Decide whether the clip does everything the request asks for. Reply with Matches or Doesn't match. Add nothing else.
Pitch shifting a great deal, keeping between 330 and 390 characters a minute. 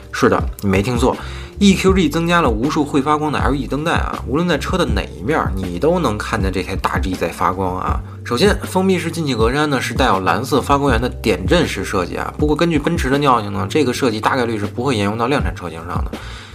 Matches